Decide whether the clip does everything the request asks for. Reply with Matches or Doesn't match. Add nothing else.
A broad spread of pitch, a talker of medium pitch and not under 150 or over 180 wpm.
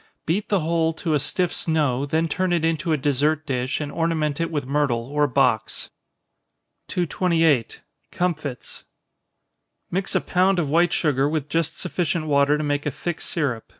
Doesn't match